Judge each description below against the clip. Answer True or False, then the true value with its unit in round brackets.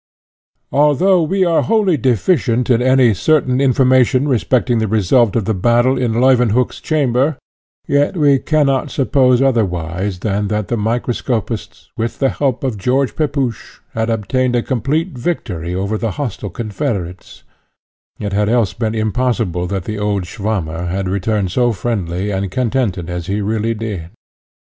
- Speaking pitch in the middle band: False (115 Hz)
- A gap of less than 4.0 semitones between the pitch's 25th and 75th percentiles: False (4.5 semitones)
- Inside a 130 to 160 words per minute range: True (150 wpm)